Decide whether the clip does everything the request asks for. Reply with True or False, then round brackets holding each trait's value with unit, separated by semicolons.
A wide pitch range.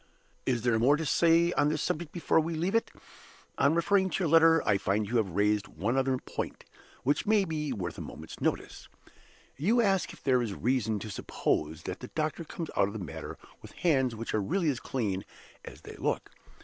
True (7.2 semitones)